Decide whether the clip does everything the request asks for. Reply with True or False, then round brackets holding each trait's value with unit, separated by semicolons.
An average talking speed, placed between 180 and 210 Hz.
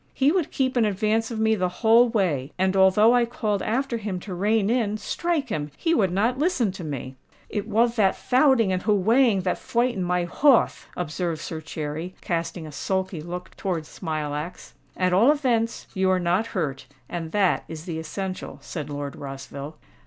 True (175 wpm; 190 Hz)